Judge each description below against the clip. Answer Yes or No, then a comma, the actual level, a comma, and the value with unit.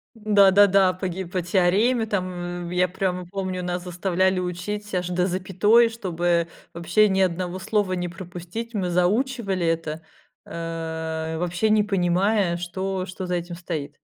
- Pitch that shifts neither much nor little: No, narrow, 2.1 semitones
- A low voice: No, medium, 180 Hz